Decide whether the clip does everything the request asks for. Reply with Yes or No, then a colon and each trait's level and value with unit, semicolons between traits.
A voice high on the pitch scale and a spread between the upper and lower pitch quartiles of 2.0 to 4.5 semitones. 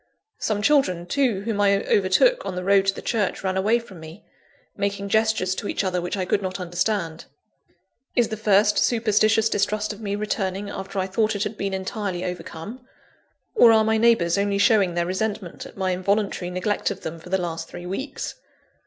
Yes: high, 200 Hz; average, 2.8 semitones